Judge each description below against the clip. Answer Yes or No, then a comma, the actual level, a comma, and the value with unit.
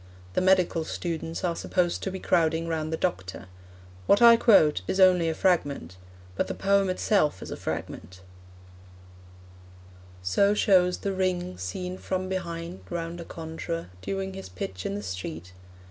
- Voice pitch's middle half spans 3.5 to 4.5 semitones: Yes, average, 4.0 semitones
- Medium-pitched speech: Yes, medium, 170 Hz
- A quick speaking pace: No, average, 155 wpm